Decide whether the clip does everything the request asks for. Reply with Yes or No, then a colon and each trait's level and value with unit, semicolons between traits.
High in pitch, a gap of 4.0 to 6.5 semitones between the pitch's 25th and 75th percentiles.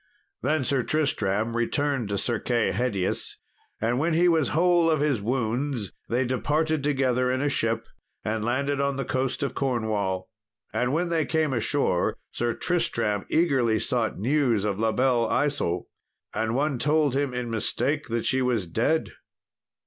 No: low, 130 Hz; average, 4.3 semitones